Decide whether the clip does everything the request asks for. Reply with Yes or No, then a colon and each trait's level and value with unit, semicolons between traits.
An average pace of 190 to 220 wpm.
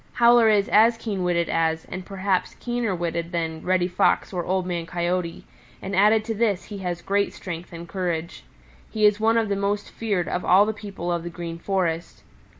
Yes: average, 200 wpm